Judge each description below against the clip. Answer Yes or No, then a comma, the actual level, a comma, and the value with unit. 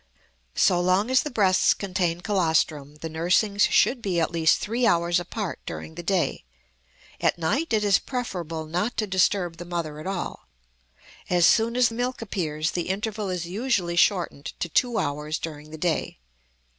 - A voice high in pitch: No, medium, 180 Hz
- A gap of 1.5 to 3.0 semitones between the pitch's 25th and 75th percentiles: No, average, 4.2 semitones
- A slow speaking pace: No, average, 170 wpm